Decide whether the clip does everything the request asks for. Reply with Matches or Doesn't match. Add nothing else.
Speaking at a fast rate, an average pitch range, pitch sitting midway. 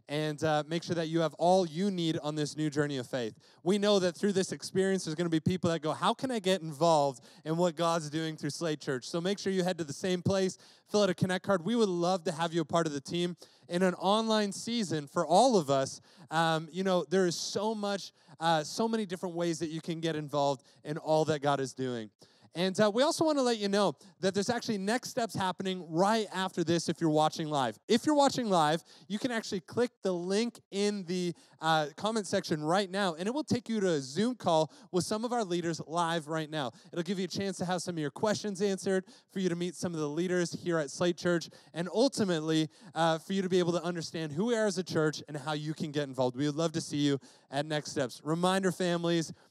Matches